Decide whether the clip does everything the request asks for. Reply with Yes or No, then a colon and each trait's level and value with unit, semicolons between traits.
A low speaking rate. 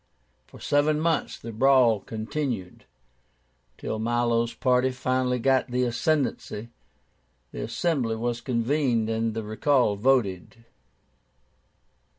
Yes: slow, 105 wpm